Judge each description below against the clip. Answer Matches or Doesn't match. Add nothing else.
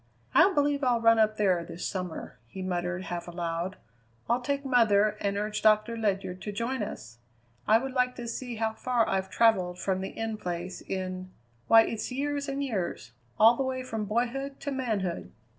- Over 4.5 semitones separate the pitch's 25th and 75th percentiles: Matches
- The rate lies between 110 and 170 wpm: Doesn't match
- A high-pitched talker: Matches